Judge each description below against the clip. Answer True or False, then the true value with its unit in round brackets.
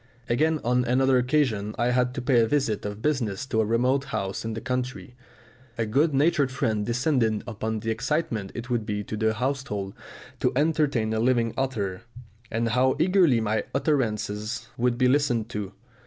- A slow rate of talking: False (175 wpm)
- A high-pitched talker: False (120 Hz)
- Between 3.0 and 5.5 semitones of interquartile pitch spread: True (3.5 semitones)